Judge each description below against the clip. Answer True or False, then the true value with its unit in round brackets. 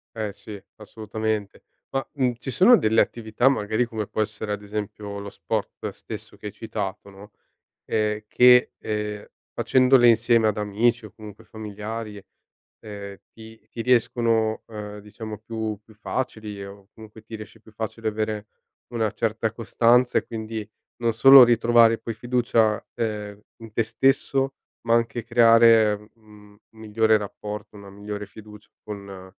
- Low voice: True (110 Hz)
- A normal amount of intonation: False (1.8 semitones)